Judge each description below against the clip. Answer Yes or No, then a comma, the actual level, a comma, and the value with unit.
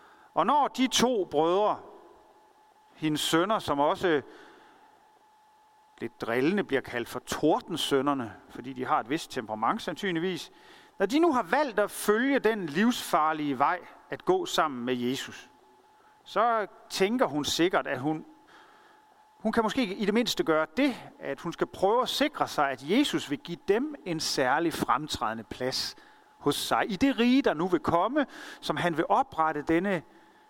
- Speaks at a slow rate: No, average, 160 wpm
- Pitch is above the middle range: Yes, high, 220 Hz